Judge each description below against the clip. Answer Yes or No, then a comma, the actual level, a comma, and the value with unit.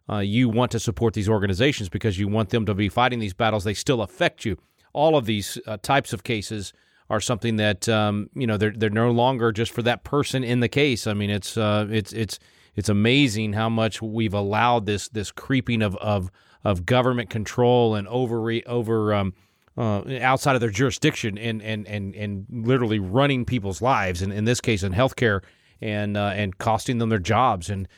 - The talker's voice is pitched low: Yes, low, 110 Hz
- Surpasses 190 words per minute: Yes, fast, 205 wpm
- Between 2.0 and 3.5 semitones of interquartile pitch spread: Yes, narrow, 2.6 semitones